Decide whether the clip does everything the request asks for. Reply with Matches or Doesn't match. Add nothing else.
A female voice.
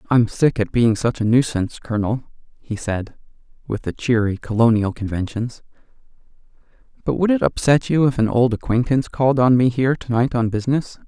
Doesn't match